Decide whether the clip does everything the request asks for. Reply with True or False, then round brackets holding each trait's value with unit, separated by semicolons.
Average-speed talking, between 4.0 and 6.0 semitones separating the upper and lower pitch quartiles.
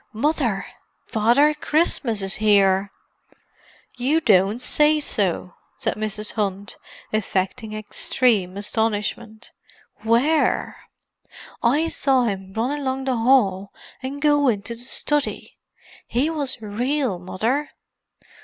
False (105 wpm; 5.2 semitones)